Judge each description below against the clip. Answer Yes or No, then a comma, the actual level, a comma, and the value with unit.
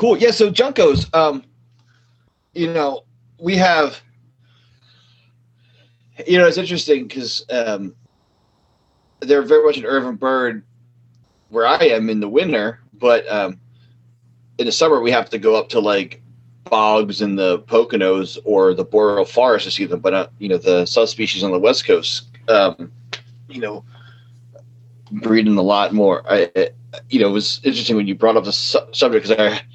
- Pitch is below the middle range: Yes, low, 120 Hz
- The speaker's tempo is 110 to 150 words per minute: No, average, 165 wpm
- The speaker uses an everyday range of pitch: Yes, average, 3.8 semitones